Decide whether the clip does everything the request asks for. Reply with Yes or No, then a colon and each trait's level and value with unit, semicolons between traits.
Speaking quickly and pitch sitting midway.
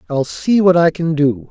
Yes: fast, 240 wpm; medium, 160 Hz